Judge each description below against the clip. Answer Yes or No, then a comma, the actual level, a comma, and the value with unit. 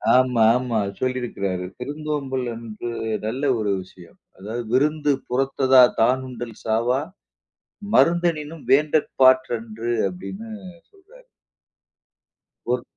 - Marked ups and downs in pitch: No, average, 4.3 semitones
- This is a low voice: Yes, low, 130 Hz